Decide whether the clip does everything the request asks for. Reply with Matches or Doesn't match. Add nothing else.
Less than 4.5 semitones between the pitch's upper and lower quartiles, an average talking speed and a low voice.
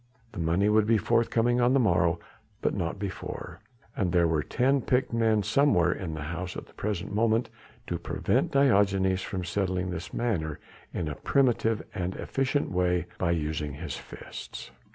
Doesn't match